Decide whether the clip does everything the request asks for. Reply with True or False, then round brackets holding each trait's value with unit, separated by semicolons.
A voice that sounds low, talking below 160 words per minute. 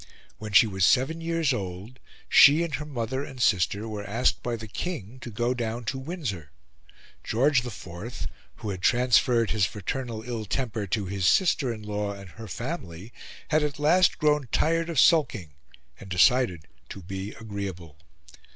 False (115 Hz; 165 wpm)